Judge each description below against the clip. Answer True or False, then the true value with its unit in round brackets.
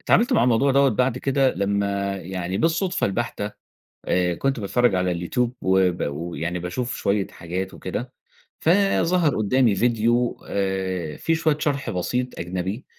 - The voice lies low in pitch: True (105 Hz)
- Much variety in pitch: True (6.0 semitones)